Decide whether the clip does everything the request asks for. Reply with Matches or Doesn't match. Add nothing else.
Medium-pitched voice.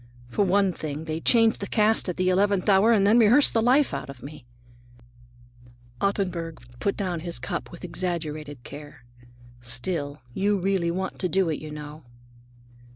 Matches